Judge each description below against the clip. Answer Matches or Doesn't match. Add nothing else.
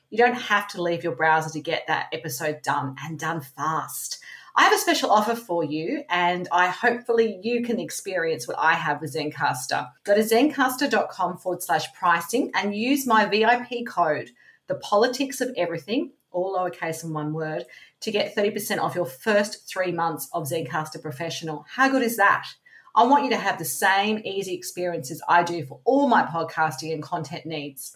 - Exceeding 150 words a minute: Matches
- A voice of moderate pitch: Matches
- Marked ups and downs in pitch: Matches